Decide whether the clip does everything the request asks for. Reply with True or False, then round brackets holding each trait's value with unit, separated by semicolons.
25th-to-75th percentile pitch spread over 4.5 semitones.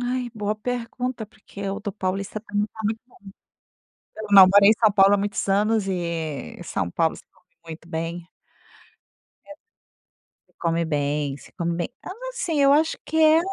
True (5.3 semitones)